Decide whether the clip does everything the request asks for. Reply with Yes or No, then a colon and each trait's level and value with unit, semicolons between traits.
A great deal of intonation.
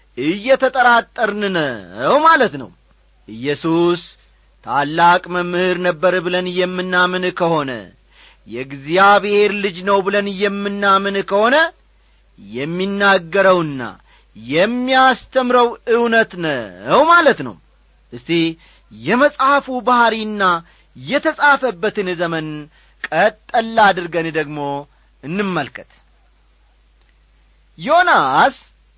Yes: wide, 6.2 semitones